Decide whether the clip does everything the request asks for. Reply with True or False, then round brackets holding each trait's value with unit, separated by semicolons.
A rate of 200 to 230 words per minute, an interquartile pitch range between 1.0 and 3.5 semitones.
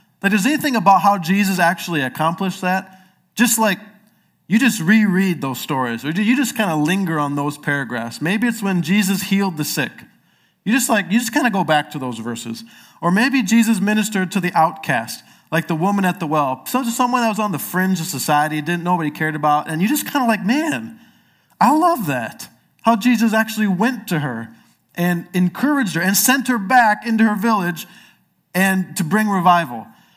False (205 wpm; 5.4 semitones)